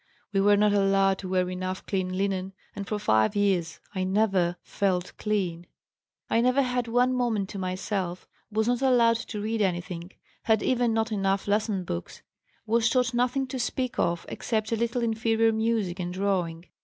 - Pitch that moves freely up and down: No, average, 3.7 semitones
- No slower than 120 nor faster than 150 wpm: No, average, 175 wpm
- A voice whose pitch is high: Yes, high, 205 Hz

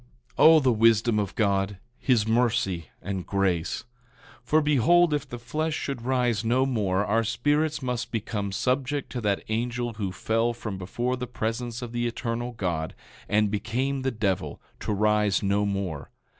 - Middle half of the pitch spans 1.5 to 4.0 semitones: Yes, average, 3.7 semitones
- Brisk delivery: No, average, 165 wpm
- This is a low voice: Yes, low, 115 Hz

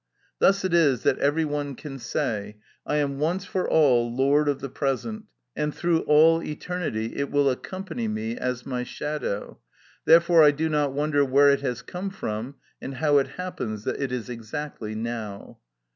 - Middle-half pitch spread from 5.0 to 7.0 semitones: No, average, 4.3 semitones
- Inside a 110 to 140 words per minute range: No, average, 175 wpm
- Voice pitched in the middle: Yes, medium, 145 Hz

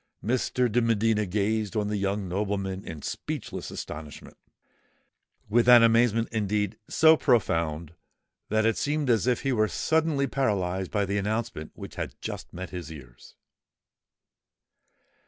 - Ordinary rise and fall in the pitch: Yes, average, 3.8 semitones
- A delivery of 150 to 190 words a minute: No, slow, 135 wpm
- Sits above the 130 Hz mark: No, low, 105 Hz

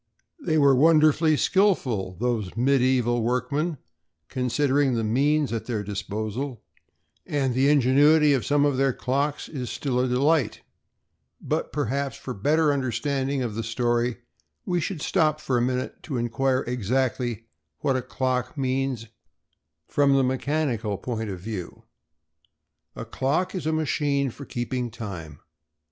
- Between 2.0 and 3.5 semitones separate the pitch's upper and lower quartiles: Yes, average, 3.2 semitones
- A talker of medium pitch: No, low, 130 Hz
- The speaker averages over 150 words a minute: No, average, 140 wpm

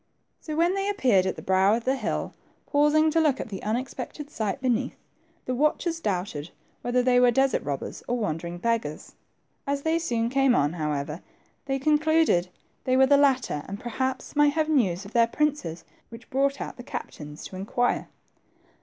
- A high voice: Yes, very high, 250 Hz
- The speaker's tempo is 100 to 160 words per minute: No, average, 185 wpm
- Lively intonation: Yes, wide, 6.5 semitones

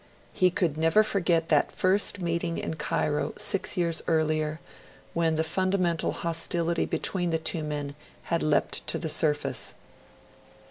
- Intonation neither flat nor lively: No, narrow, 2.1 semitones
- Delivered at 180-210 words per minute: No, average, 140 wpm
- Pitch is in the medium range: Yes, medium, 165 Hz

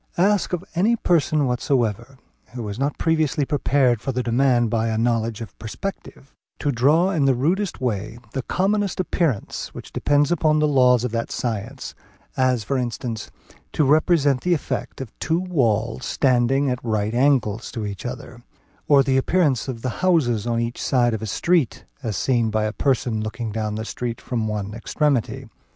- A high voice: No, low, 125 Hz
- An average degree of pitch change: Yes, average, 4.3 semitones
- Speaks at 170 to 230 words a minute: Yes, average, 175 wpm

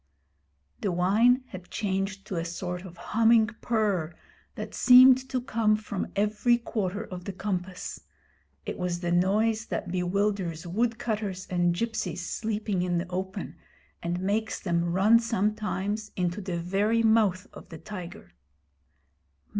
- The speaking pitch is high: Yes, high, 195 Hz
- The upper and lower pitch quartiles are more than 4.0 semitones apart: No, average, 3.5 semitones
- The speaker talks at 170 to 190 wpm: No, average, 140 wpm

